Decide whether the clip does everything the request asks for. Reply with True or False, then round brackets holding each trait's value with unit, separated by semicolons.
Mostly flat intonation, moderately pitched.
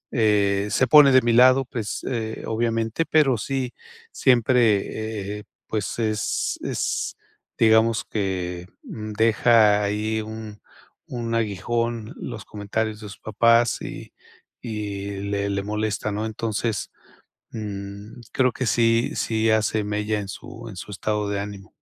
False (2.0 semitones; 110 Hz)